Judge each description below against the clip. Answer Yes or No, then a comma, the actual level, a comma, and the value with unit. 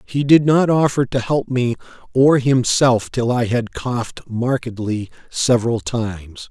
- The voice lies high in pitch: No, low, 125 Hz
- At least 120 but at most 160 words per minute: Yes, average, 150 wpm